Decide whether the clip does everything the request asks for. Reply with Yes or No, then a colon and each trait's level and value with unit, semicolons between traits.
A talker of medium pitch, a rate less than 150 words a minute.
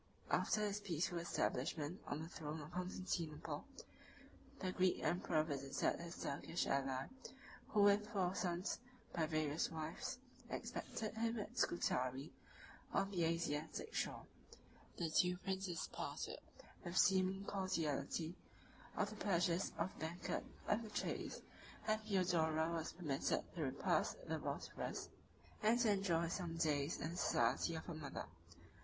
Yes: medium, 175 Hz; slow, 135 wpm